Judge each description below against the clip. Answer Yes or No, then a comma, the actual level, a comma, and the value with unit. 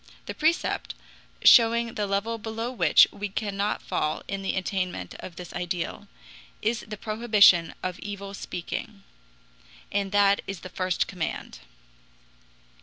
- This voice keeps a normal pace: No, slow, 130 wpm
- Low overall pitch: No, high, 200 Hz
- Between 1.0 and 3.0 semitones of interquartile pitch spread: Yes, average, 2.7 semitones